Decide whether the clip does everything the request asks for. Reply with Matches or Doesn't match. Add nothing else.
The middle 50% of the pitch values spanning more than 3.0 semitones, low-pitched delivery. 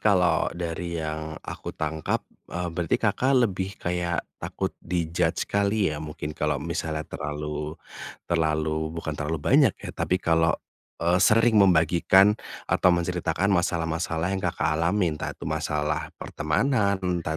Doesn't match